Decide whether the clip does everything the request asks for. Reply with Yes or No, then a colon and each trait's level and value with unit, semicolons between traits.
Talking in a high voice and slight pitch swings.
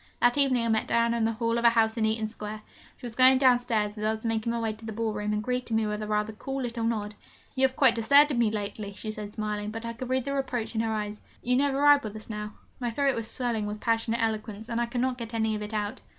Yes: high, 225 Hz; narrow, 2.3 semitones